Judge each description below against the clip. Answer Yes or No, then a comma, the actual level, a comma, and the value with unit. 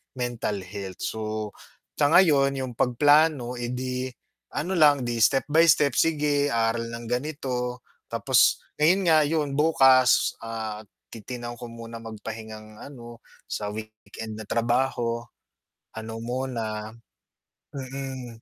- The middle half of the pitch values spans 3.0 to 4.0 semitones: Yes, average, 3.5 semitones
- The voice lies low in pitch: Yes, low, 125 Hz